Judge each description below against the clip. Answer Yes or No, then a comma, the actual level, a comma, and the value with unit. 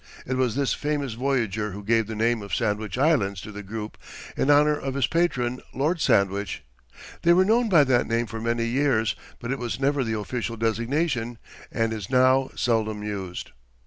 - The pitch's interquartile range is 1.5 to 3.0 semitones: No, average, 4.1 semitones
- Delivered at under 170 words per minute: No, average, 185 wpm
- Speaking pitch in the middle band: No, low, 120 Hz